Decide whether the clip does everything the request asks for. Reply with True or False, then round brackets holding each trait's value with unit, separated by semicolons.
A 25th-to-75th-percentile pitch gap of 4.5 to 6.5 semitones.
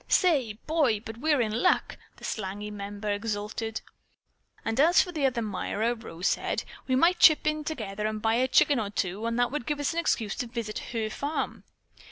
True (5.3 semitones)